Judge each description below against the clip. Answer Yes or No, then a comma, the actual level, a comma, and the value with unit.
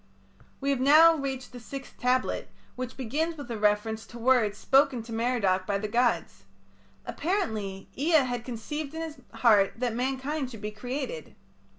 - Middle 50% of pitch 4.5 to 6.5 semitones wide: No, average, 4.0 semitones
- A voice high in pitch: Yes, very high, 250 Hz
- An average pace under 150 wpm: No, average, 165 wpm